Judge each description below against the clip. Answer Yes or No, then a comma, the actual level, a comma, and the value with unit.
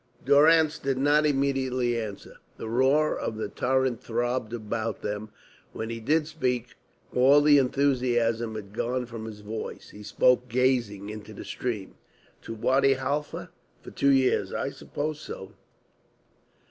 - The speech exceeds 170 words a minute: No, average, 145 wpm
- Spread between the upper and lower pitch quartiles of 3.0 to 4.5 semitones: Yes, average, 3.6 semitones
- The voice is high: No, low, 125 Hz